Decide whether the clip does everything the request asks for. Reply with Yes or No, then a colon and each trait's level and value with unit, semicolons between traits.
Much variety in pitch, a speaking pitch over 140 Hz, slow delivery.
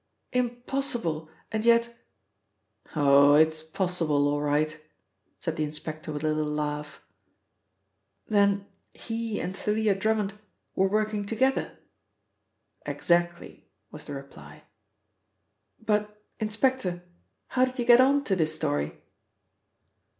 Yes: wide, 6.3 semitones; high, 190 Hz; slow, 115 wpm